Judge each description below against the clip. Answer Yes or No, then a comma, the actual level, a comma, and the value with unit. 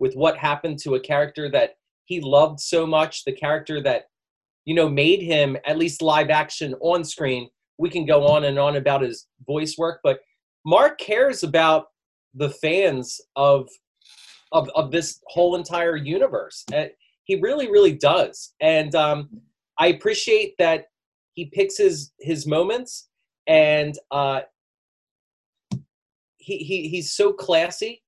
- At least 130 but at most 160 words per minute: Yes, average, 145 wpm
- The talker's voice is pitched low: No, medium, 160 Hz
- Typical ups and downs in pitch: Yes, average, 4.6 semitones